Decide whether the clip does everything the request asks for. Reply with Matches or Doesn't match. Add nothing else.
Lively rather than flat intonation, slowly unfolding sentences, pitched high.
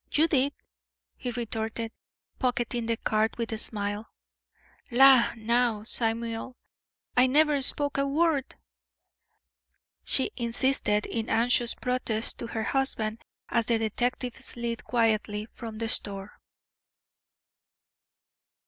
Doesn't match